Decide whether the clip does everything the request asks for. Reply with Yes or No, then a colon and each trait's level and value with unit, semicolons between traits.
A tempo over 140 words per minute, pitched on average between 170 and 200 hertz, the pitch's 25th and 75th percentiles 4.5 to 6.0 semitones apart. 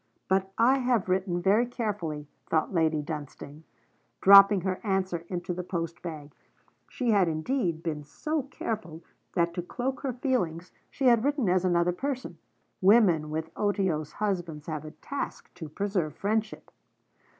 Yes: average, 150 wpm; medium, 185 Hz; average, 5.1 semitones